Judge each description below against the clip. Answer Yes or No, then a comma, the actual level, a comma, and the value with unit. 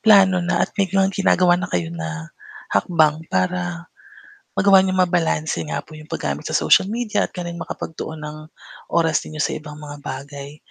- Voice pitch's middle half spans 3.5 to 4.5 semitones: Yes, average, 4.0 semitones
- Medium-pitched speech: Yes, medium, 165 Hz